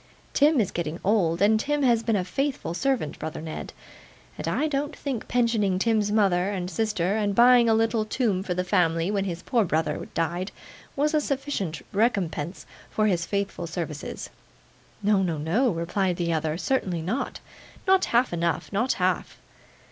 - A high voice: Yes, high, 200 Hz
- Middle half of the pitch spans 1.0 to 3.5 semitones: No, wide, 5.4 semitones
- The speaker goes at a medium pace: Yes, average, 170 wpm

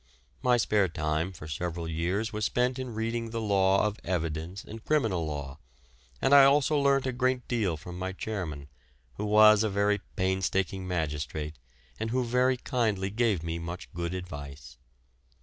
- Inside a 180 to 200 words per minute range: No, average, 165 wpm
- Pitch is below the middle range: Yes, very low, 95 Hz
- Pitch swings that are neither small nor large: No, wide, 5.7 semitones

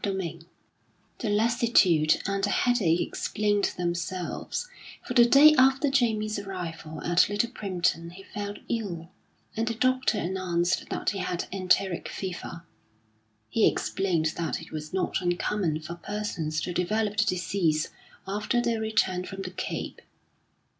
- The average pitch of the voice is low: No, high, 195 Hz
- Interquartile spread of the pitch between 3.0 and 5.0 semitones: Yes, average, 3.8 semitones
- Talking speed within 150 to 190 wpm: No, average, 140 wpm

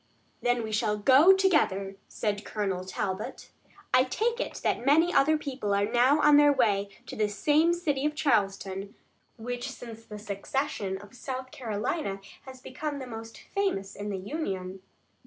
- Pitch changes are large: Yes, wide, 6.2 semitones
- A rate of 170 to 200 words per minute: No, average, 160 wpm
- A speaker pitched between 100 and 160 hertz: No, high, 240 Hz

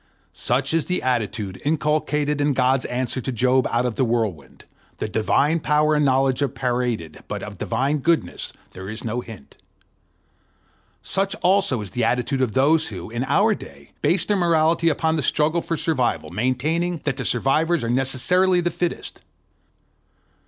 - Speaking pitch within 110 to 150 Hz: Yes, low, 135 Hz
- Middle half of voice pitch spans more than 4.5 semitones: Yes, average, 4.9 semitones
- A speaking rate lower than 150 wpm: No, average, 170 wpm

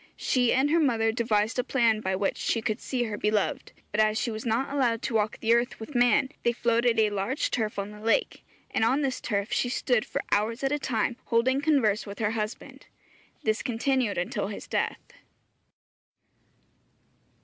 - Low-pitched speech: No, high, 230 Hz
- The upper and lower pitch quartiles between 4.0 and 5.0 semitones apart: No, average, 2.8 semitones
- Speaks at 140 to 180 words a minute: No, average, 190 wpm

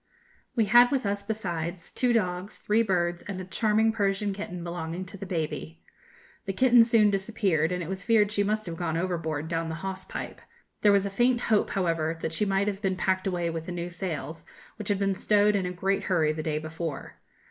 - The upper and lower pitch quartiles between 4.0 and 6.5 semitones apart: No, average, 3.5 semitones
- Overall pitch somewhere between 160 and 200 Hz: Yes, high, 190 Hz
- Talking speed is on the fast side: Yes, fast, 215 wpm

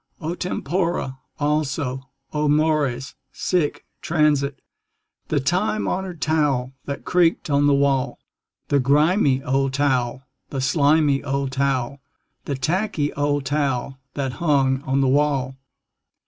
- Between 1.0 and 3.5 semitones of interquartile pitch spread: Yes, narrow, 2.4 semitones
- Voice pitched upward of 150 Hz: No, medium, 140 Hz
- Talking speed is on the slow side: Yes, slow, 120 wpm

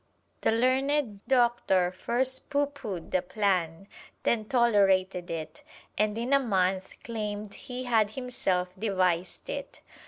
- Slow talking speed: Yes, slow, 125 wpm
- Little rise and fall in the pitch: No, average, 4.9 semitones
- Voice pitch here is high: Yes, high, 210 Hz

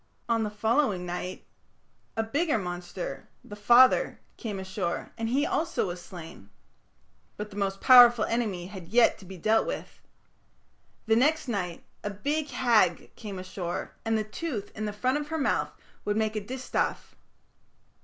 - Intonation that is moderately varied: Yes, average, 4.3 semitones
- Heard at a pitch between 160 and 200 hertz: No, high, 215 Hz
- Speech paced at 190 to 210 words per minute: No, average, 160 wpm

